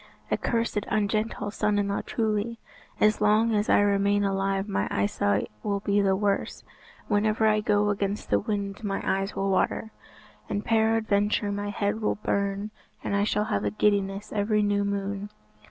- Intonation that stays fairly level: Yes, narrow, 1.1 semitones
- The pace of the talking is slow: No, average, 170 wpm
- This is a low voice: No, high, 205 Hz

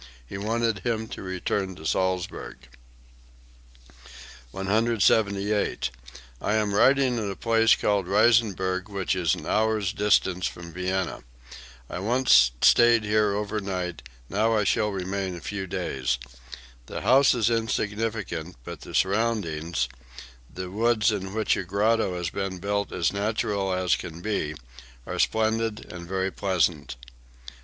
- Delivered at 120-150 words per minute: Yes, slow, 135 wpm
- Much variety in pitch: No, average, 3.0 semitones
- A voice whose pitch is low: Yes, low, 100 Hz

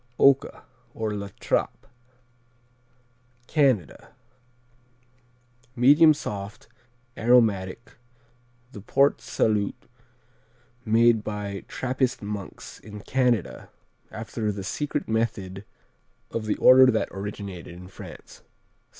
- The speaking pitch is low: Yes, low, 110 Hz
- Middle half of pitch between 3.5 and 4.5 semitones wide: Yes, average, 3.8 semitones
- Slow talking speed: Yes, slow, 90 wpm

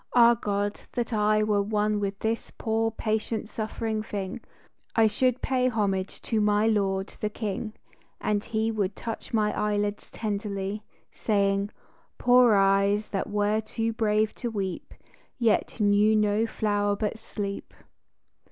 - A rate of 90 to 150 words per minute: Yes, average, 145 wpm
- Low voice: No, high, 210 Hz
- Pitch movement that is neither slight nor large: No, narrow, 1.5 semitones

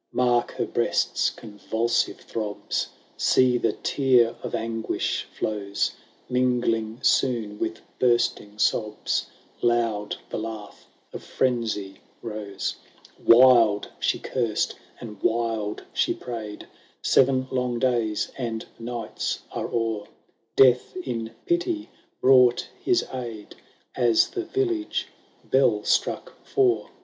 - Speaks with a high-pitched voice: No, low, 115 Hz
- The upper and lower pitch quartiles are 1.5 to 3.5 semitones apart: Yes, average, 2.7 semitones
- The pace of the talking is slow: Yes, slow, 110 wpm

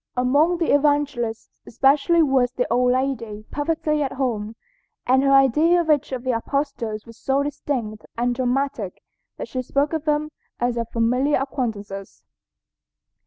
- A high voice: Yes, very high, 265 Hz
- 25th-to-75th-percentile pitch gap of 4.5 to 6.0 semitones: No, average, 3.6 semitones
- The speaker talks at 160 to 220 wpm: No, average, 150 wpm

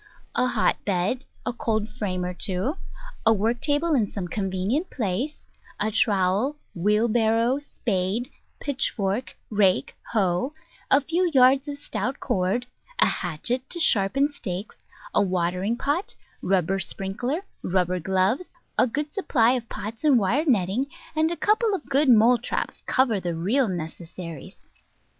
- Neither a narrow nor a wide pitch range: No, wide, 6.2 semitones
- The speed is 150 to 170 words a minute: No, average, 140 wpm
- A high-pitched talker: Yes, high, 225 Hz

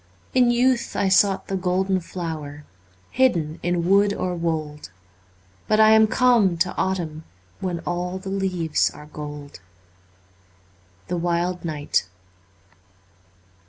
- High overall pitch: No, medium, 175 Hz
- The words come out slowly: Yes, slow, 125 wpm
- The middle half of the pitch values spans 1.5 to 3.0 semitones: No, average, 4.0 semitones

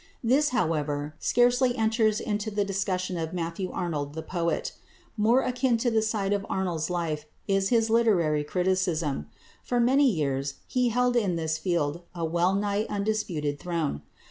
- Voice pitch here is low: No, high, 190 Hz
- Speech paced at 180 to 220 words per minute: No, average, 155 wpm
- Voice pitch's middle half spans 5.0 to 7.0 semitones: Yes, wide, 5.5 semitones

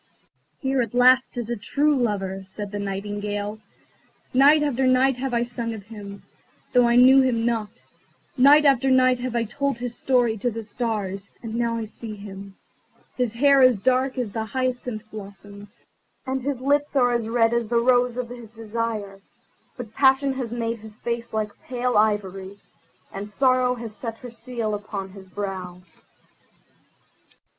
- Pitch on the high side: Yes, high, 235 Hz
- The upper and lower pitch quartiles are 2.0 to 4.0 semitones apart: Yes, average, 3.5 semitones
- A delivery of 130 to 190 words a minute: Yes, average, 165 wpm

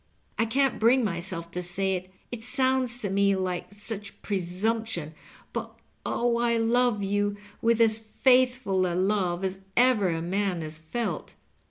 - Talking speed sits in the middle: Yes, average, 165 wpm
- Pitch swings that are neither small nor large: Yes, average, 4.1 semitones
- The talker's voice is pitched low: No, high, 205 Hz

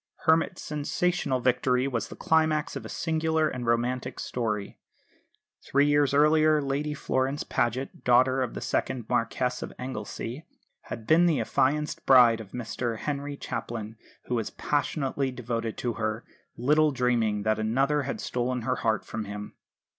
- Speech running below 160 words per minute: Yes, average, 150 wpm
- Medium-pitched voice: No, low, 130 Hz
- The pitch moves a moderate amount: Yes, average, 4.0 semitones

